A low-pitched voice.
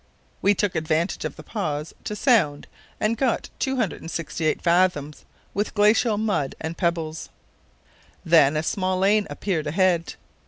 No: medium, 175 Hz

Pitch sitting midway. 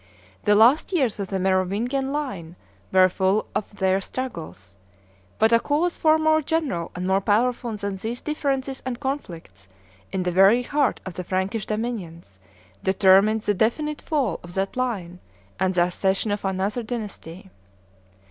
No: high, 205 Hz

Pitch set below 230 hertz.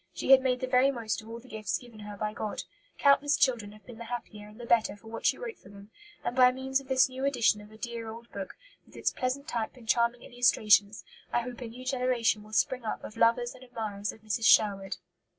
No: high, 235 Hz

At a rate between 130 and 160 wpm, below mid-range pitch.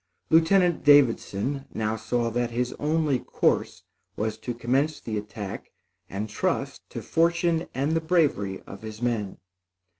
Yes: average, 140 wpm; low, 125 Hz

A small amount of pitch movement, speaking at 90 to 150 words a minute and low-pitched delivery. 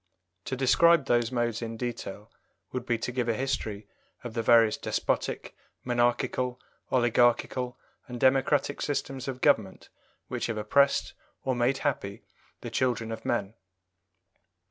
Yes: narrow, 2.3 semitones; slow, 135 wpm; low, 120 Hz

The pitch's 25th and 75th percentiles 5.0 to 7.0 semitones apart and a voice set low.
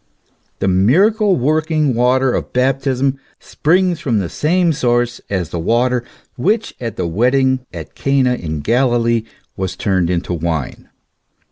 Yes: wide, 5.6 semitones; low, 125 Hz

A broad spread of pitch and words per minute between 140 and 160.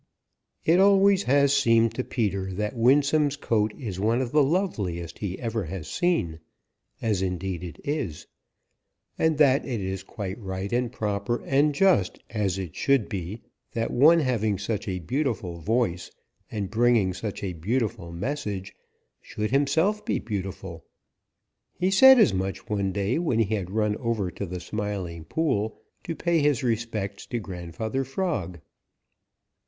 Yes: wide, 6.2 semitones; average, 150 wpm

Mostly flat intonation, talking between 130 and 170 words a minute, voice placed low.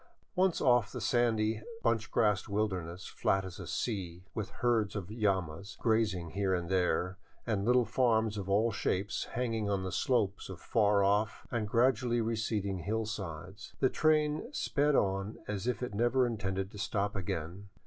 No: average, 3.3 semitones; average, 165 wpm; low, 105 Hz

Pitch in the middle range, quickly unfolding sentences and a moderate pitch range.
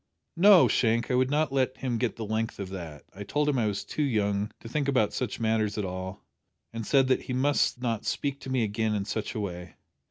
No: low, 115 Hz; fast, 245 wpm; average, 4.3 semitones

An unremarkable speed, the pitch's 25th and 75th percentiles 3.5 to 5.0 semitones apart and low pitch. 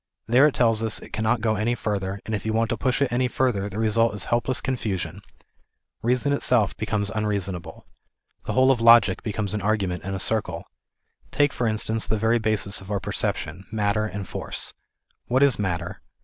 No: average, 190 wpm; average, 2.9 semitones; low, 110 Hz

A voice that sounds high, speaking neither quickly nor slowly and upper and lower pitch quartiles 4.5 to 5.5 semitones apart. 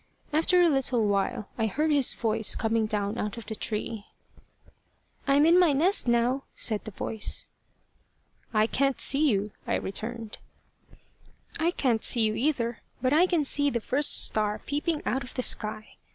Yes: high, 240 Hz; average, 170 wpm; average, 4.8 semitones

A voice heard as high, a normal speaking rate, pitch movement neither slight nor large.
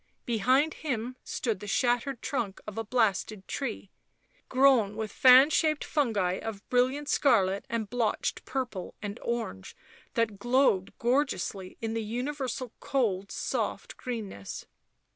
No: high, 235 Hz; slow, 125 wpm; average, 4.1 semitones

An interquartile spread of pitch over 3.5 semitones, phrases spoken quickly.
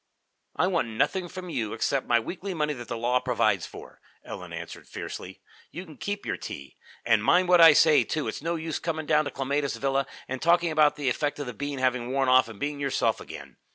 Yes: average, 4.4 semitones; fast, 225 wpm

